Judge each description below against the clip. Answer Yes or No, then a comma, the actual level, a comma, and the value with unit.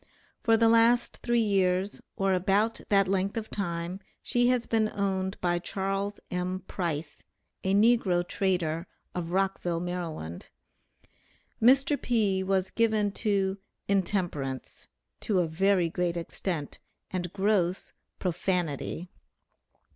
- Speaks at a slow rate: Yes, slow, 115 wpm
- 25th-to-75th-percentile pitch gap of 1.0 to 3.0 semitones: Yes, average, 2.7 semitones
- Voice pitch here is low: No, high, 190 Hz